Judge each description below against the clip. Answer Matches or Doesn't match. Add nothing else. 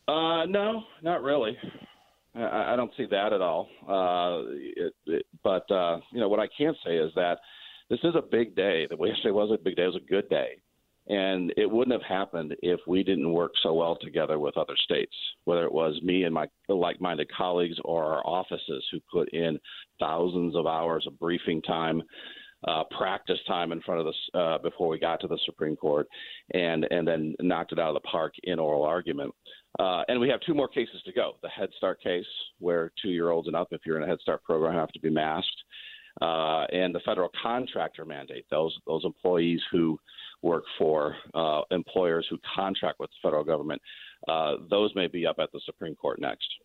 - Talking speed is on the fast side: Matches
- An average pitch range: Matches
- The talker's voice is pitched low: Matches